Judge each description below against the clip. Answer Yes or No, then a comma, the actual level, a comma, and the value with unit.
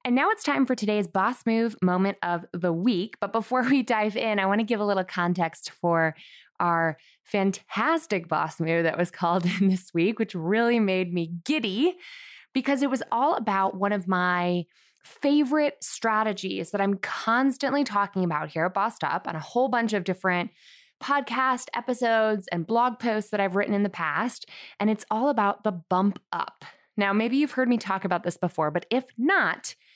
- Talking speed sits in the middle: Yes, average, 190 wpm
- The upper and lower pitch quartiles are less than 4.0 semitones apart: No, wide, 5.4 semitones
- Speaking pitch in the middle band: No, high, 205 Hz